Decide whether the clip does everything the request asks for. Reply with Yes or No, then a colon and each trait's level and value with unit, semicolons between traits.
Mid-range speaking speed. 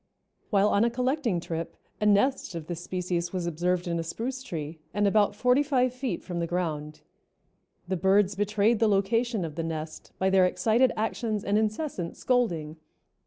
Yes: average, 175 wpm